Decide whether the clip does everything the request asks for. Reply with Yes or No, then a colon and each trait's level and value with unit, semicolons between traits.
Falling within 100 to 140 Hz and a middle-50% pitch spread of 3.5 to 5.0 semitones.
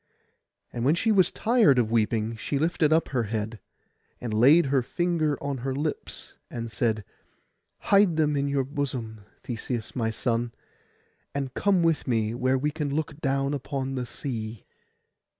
Yes: low, 135 Hz; average, 4.4 semitones